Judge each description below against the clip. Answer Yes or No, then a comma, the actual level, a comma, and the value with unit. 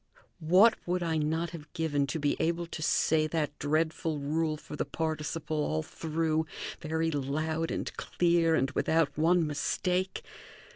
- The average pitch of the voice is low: No, medium, 160 Hz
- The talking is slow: No, average, 150 wpm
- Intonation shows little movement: Yes, narrow, 1.5 semitones